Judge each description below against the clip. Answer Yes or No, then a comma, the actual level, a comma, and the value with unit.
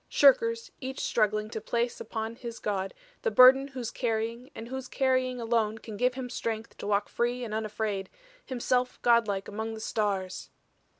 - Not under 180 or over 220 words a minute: No, average, 165 wpm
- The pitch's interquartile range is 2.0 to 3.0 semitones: Yes, average, 2.7 semitones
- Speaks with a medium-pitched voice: No, high, 230 Hz